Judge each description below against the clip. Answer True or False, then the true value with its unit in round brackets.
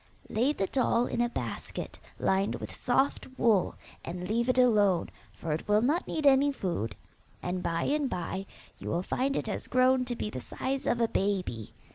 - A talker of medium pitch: False (230 Hz)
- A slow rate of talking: False (190 wpm)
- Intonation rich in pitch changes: True (5.9 semitones)